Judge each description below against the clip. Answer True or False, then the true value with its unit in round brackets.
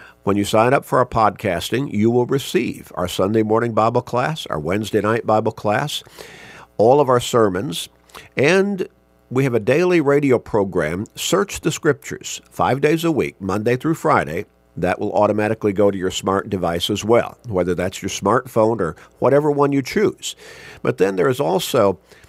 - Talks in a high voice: False (110 Hz)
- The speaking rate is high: False (175 wpm)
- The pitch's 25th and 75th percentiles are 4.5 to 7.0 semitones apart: True (5.2 semitones)